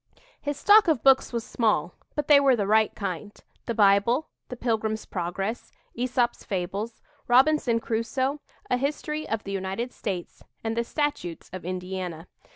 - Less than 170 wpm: Yes, average, 155 wpm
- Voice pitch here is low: No, high, 225 Hz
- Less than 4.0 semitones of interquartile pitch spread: No, average, 4.9 semitones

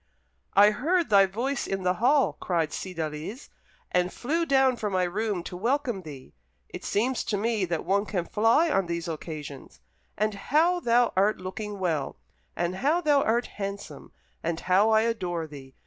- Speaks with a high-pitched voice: Yes, high, 200 Hz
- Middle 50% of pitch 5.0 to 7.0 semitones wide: Yes, wide, 5.4 semitones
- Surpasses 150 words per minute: Yes, average, 170 wpm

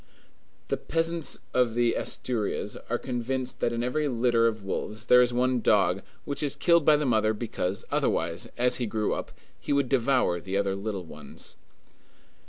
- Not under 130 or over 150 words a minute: No, average, 170 wpm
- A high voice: No, low, 120 Hz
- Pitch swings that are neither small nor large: Yes, average, 3.3 semitones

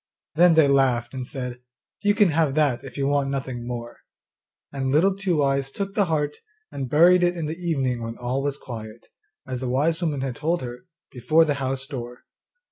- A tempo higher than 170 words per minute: Yes, average, 200 wpm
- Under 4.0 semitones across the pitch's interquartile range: No, average, 4.3 semitones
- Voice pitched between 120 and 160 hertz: Yes, medium, 140 Hz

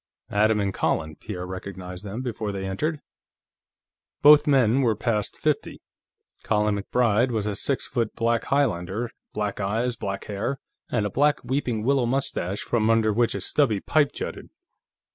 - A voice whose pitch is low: Yes, low, 110 Hz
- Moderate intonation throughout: Yes, average, 3.8 semitones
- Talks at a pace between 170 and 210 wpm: No, average, 155 wpm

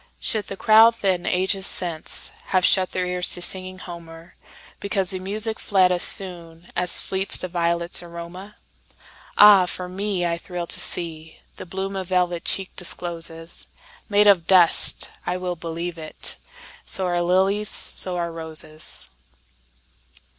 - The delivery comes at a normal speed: No, slow, 125 wpm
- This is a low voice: No, medium, 180 Hz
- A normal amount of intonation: No, narrow, 2.1 semitones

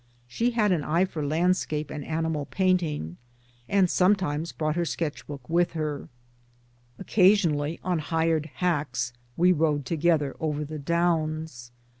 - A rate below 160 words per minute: Yes, average, 145 wpm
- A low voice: No, medium, 160 Hz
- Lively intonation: No, average, 3.0 semitones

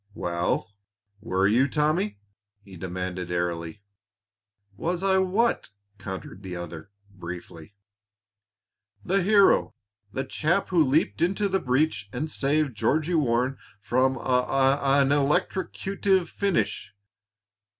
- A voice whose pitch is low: Yes, low, 130 Hz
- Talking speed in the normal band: No, slow, 110 wpm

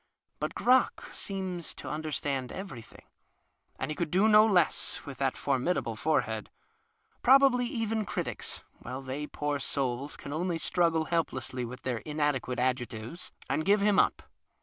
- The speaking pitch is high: No, medium, 150 Hz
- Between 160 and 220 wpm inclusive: No, average, 145 wpm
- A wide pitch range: Yes, wide, 6.4 semitones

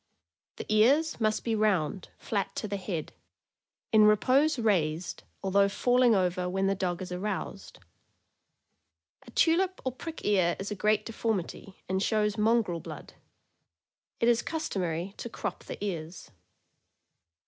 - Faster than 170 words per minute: No, slow, 135 wpm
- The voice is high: Yes, high, 205 Hz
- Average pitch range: Yes, average, 3.7 semitones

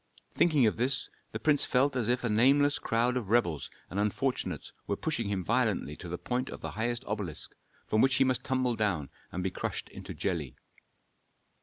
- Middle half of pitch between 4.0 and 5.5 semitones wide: Yes, average, 4.7 semitones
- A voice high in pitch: No, low, 115 Hz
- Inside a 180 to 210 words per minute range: Yes, average, 190 wpm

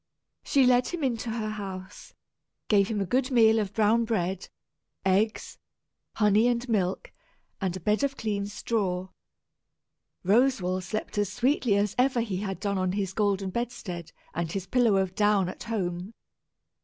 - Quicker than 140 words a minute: Yes, average, 155 wpm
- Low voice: No, high, 205 Hz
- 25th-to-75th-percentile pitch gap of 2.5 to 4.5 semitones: Yes, average, 3.5 semitones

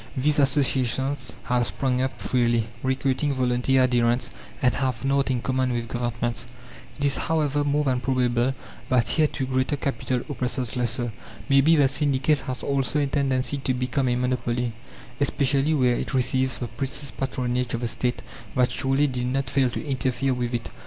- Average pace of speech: Yes, average, 170 wpm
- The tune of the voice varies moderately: No, narrow, 1.9 semitones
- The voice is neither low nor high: No, low, 130 Hz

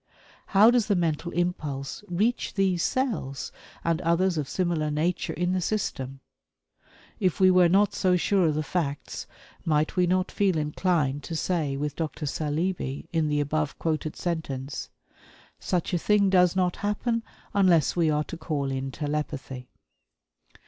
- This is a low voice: No, medium, 170 Hz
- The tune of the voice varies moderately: Yes, average, 3.8 semitones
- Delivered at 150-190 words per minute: Yes, average, 155 wpm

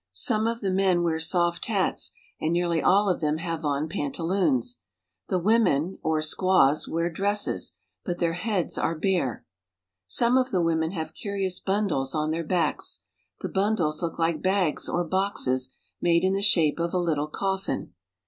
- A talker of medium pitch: Yes, medium, 175 Hz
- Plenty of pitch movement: No, average, 3.5 semitones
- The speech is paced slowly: No, average, 165 wpm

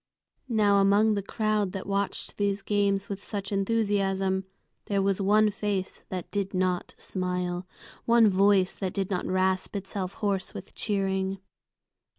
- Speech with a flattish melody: Yes, narrow, 1.3 semitones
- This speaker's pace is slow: No, average, 145 wpm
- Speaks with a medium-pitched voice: No, high, 195 Hz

